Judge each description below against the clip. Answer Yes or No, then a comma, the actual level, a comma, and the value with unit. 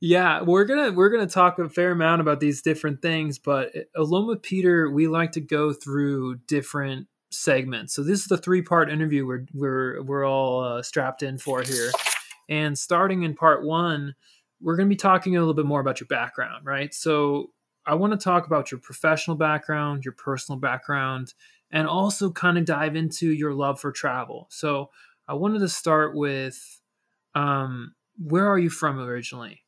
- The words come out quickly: No, average, 190 wpm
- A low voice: No, medium, 155 Hz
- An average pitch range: Yes, average, 3.7 semitones